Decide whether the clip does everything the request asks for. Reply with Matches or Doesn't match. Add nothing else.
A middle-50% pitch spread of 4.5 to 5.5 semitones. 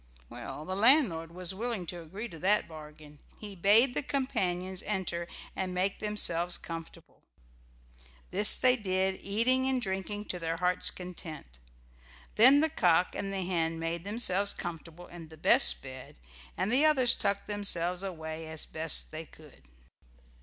Doesn't match